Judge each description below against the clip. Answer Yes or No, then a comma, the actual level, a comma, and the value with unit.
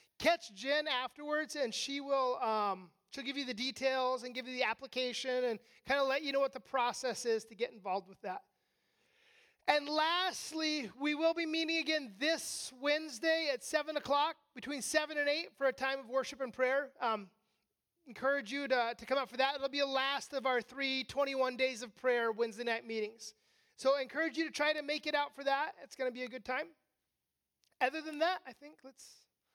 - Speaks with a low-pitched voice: No, very high, 270 Hz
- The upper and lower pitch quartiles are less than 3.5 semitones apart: Yes, average, 3.0 semitones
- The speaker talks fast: Yes, fast, 210 wpm